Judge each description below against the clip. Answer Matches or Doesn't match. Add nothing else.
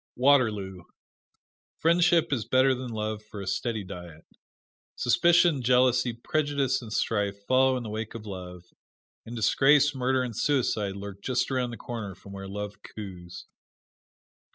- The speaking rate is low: Doesn't match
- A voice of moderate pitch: Doesn't match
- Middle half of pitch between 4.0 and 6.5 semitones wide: Matches